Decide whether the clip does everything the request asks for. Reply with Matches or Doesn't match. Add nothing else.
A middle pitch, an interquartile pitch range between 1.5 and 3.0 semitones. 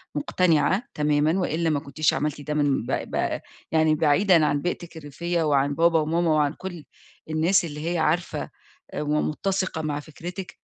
Matches